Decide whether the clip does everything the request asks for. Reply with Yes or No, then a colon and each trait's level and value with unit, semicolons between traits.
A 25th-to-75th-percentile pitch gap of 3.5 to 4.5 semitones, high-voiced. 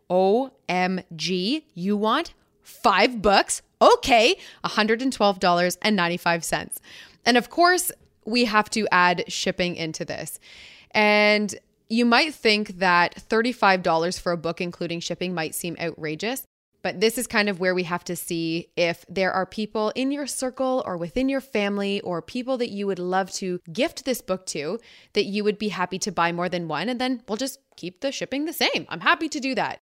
No: wide, 5.4 semitones; high, 205 Hz